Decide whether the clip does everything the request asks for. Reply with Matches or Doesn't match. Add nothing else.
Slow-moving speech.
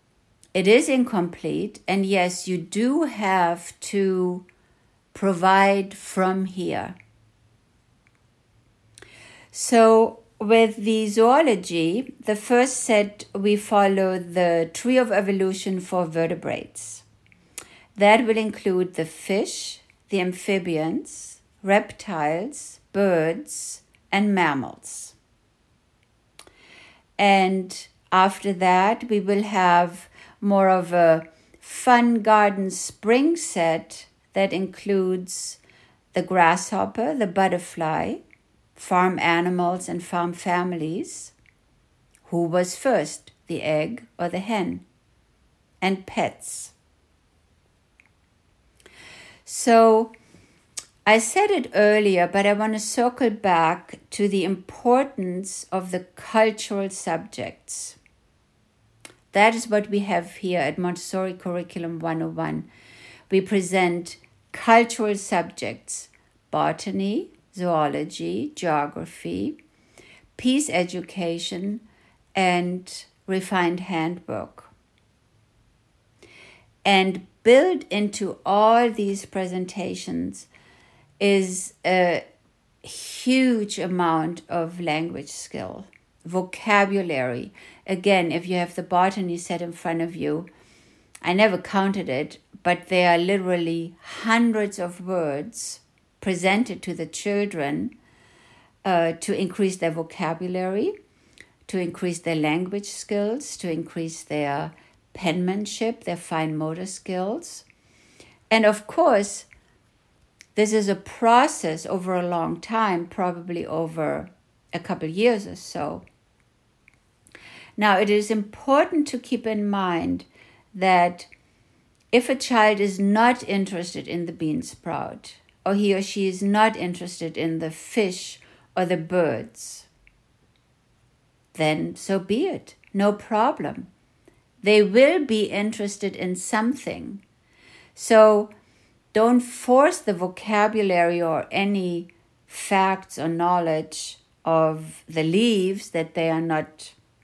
Matches